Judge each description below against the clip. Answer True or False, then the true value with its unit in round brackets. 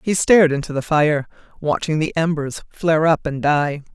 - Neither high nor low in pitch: True (155 Hz)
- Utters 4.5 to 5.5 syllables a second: True (5.0 syllables/s)